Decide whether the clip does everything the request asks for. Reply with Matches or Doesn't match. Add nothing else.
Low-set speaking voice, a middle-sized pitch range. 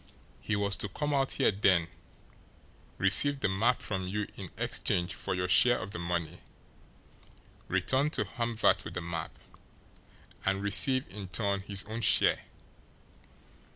Matches